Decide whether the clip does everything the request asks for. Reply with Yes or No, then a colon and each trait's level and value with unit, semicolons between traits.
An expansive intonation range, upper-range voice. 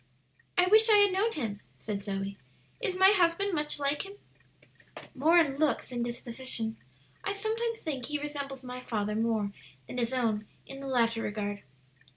Yes: wide, 8.0 semitones; very high, 270 Hz